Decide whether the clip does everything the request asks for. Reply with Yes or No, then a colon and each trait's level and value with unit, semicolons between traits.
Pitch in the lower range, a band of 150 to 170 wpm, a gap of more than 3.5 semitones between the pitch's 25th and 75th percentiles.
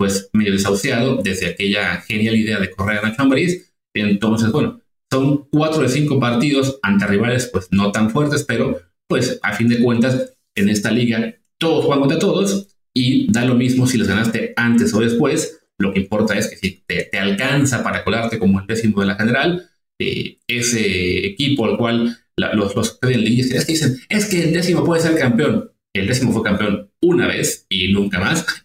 No: low, 115 Hz; average, 190 wpm; average, 4.7 semitones